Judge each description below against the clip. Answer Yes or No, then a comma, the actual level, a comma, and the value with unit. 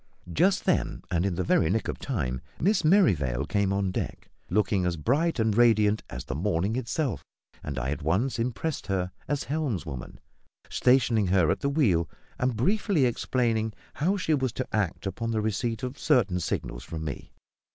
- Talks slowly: No, average, 175 wpm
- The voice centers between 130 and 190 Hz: No, low, 110 Hz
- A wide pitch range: Yes, wide, 6.5 semitones